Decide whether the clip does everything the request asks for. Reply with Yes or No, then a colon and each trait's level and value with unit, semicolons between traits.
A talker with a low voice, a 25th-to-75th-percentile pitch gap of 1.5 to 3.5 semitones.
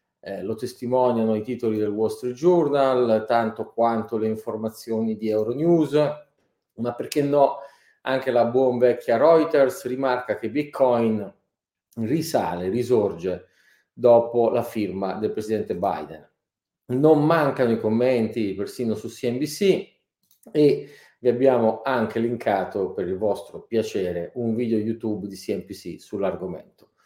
Yes: low, 120 Hz; average, 3.2 semitones